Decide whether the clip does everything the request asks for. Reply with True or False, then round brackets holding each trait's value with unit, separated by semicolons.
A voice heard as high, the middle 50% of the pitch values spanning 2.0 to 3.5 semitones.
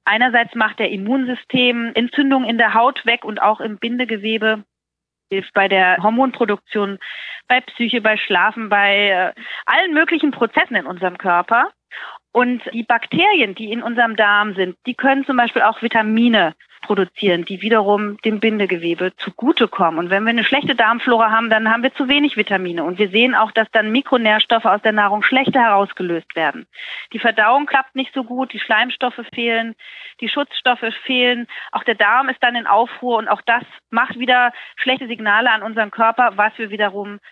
True (230 Hz; 3.2 semitones)